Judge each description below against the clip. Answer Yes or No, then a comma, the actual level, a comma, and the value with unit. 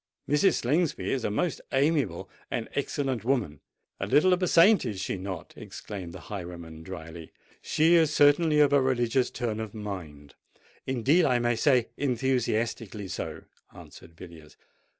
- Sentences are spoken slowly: No, average, 145 wpm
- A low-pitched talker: Yes, low, 120 Hz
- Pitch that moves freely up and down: Yes, wide, 7.4 semitones